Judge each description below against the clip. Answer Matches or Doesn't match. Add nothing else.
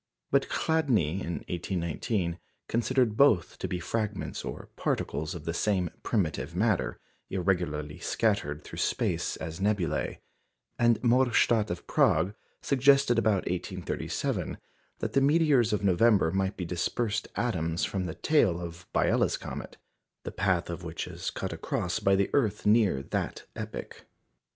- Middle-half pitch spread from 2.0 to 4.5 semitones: Doesn't match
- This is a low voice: Matches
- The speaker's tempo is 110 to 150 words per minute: Matches